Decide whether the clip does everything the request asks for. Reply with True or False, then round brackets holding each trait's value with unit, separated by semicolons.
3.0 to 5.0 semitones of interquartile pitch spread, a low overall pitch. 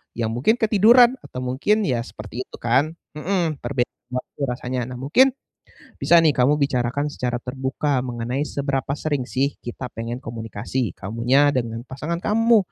True (3.8 semitones; 130 Hz)